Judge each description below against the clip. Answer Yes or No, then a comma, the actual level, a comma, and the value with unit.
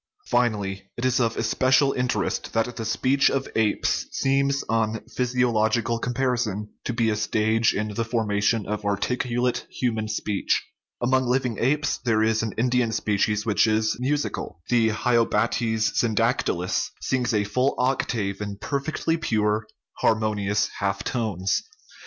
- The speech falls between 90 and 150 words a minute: Yes, average, 140 wpm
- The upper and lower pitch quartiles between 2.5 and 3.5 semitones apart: Yes, average, 2.8 semitones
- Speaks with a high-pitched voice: No, low, 115 Hz